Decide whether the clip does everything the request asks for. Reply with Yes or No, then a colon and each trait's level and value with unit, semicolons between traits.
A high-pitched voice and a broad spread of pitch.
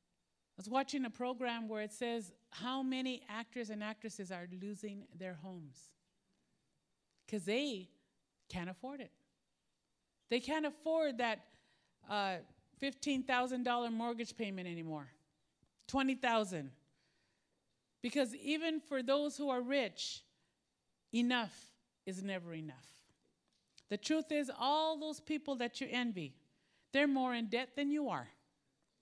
Yes: high, 235 Hz; wide, 6.1 semitones